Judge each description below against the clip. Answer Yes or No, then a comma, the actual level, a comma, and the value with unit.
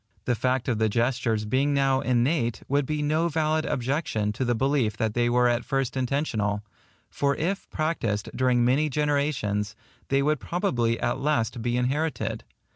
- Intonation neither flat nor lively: Yes, average, 3.8 semitones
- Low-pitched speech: Yes, low, 130 Hz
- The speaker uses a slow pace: No, average, 165 wpm